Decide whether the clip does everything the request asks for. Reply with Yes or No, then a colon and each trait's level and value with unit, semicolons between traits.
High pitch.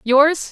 Yes: very high, 290 Hz